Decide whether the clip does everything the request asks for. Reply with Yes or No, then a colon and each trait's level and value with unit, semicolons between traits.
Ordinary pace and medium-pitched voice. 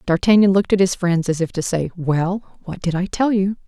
No: fast, 245 wpm; medium, 180 Hz